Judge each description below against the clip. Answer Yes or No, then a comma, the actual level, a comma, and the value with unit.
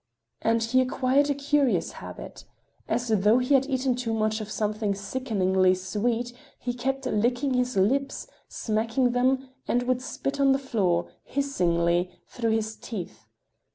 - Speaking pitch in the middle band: No, high, 240 Hz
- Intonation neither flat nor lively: Yes, average, 3.6 semitones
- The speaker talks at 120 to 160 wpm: Yes, average, 150 wpm